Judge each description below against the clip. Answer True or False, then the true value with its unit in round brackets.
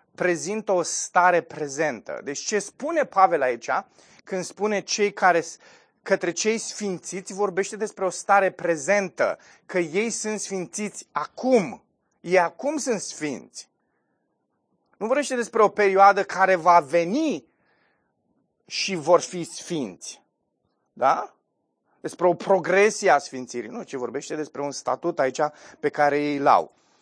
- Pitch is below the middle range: False (190 Hz)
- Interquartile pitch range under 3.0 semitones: False (3.7 semitones)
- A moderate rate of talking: True (135 wpm)